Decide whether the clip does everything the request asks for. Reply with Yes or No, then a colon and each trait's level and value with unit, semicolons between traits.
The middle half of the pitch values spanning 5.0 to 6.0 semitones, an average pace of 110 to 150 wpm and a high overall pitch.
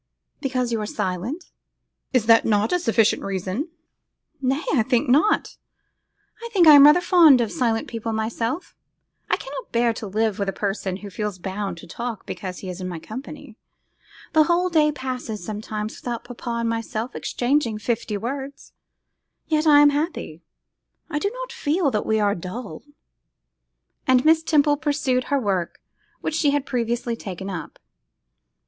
No: wide, 5.6 semitones; average, 165 wpm; high, 235 Hz